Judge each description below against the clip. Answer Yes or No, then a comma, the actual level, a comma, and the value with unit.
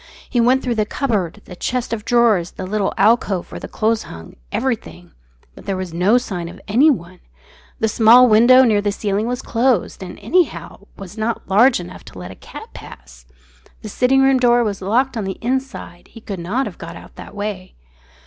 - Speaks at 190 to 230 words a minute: Yes, average, 195 wpm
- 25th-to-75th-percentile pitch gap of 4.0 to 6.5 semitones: Yes, average, 4.5 semitones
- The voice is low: No, high, 215 Hz